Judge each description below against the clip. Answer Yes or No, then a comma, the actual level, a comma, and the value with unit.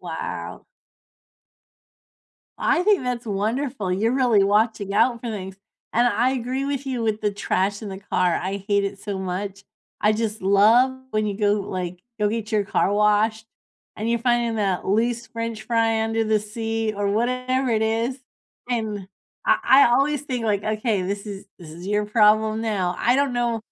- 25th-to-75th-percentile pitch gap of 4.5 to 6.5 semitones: No, average, 2.8 semitones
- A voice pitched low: No, high, 220 Hz